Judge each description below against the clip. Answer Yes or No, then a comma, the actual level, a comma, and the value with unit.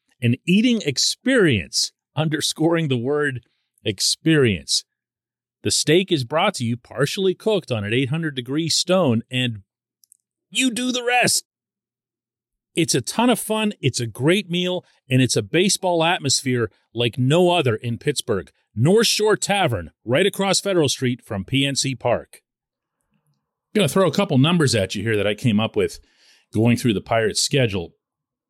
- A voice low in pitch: No, medium, 145 Hz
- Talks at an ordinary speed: Yes, average, 155 wpm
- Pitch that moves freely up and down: Yes, wide, 7.1 semitones